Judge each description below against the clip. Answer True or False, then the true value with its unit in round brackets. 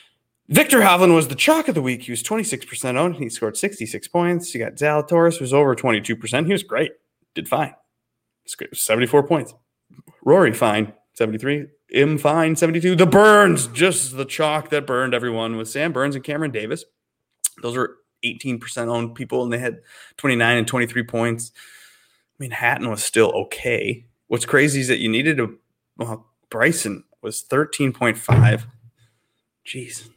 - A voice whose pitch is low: True (130 Hz)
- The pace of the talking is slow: False (160 wpm)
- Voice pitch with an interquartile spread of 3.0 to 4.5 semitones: False (5.2 semitones)